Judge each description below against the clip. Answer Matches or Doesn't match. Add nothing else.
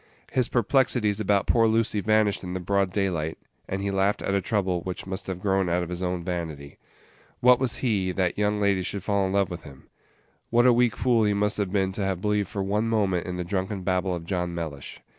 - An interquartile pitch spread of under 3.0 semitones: Matches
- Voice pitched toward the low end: Matches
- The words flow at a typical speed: Doesn't match